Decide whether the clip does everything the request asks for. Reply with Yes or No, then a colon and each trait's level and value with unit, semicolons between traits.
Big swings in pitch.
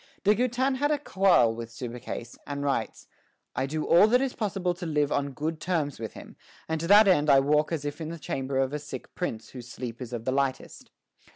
Yes: wide, 5.7 semitones